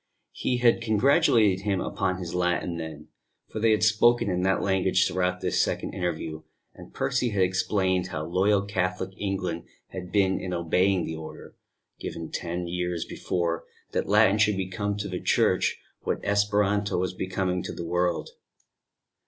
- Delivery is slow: No, average, 160 wpm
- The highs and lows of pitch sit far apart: No, narrow, 2.4 semitones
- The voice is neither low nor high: No, very low, 95 Hz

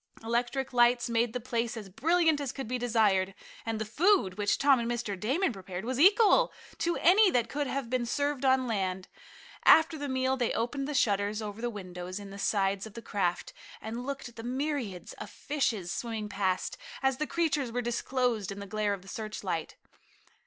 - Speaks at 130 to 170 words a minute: No, average, 195 wpm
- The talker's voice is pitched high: Yes, high, 235 Hz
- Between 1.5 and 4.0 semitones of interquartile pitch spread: No, average, 4.7 semitones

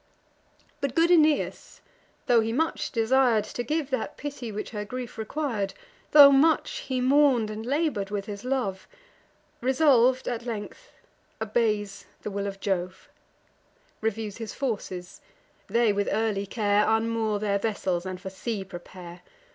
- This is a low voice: No, high, 225 Hz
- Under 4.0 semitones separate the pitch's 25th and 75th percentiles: No, average, 4.3 semitones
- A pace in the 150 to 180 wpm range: No, average, 140 wpm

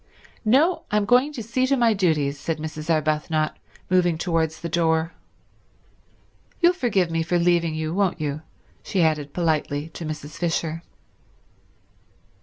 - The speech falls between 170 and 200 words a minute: No, average, 140 wpm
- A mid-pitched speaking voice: Yes, medium, 165 Hz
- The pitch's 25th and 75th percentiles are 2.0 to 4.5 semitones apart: Yes, average, 4.2 semitones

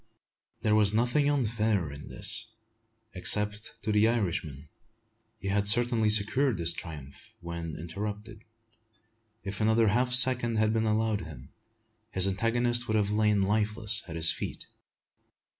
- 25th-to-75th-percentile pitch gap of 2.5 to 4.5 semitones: Yes, average, 2.8 semitones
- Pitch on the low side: Yes, low, 105 Hz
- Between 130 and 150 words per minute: Yes, average, 140 wpm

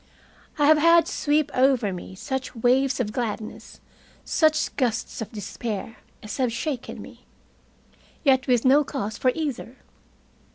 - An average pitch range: Yes, average, 4.4 semitones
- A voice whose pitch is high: Yes, very high, 255 Hz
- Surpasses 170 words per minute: No, slow, 135 wpm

